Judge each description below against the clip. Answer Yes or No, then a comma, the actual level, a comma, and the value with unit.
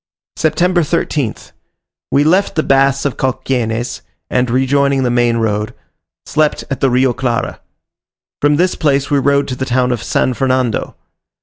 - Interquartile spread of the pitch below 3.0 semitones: Yes, narrow, 2.4 semitones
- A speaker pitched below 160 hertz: Yes, low, 135 Hz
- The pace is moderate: Yes, average, 150 wpm